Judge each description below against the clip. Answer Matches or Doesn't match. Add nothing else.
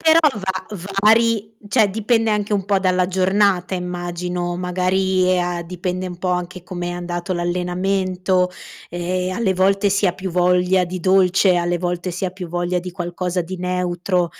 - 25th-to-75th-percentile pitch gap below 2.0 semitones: Matches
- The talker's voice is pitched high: Doesn't match